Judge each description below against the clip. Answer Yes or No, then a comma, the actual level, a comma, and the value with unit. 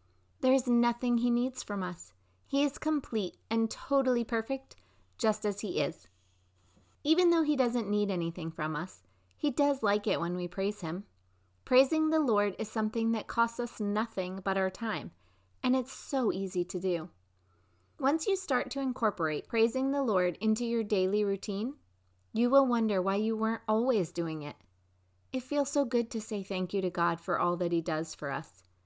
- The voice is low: No, high, 205 Hz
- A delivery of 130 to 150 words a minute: No, average, 185 wpm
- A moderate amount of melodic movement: No, wide, 6.7 semitones